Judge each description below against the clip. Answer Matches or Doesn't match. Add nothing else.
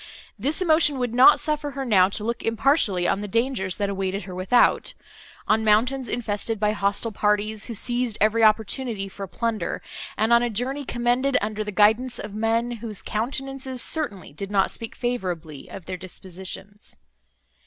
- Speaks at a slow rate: Doesn't match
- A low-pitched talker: Doesn't match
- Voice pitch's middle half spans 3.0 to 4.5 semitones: Matches